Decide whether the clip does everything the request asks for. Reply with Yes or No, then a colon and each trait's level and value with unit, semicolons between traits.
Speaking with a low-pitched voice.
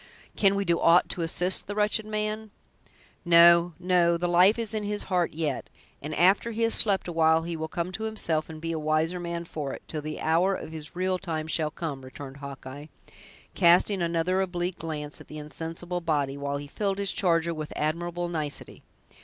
No: medium, 170 Hz